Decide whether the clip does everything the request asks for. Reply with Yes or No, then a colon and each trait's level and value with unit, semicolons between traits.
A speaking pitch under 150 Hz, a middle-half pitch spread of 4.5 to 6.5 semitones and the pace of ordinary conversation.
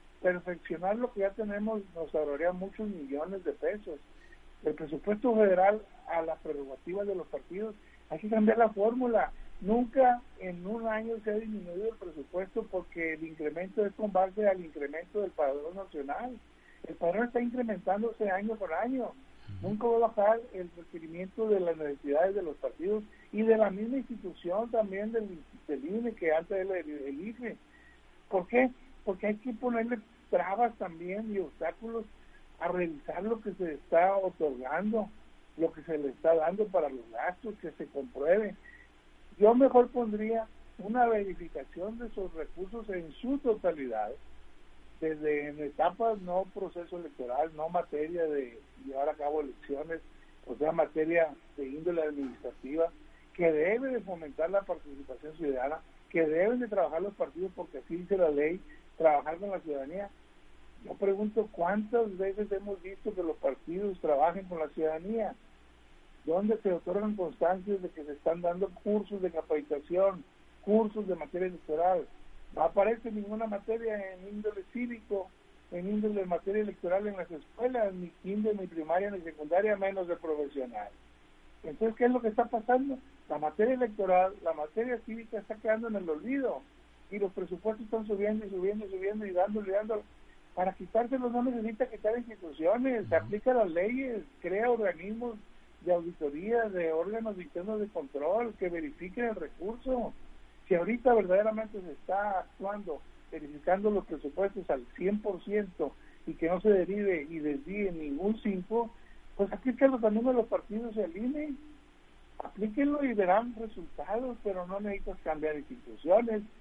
No: high, 195 Hz; average, 5.1 semitones; average, 155 wpm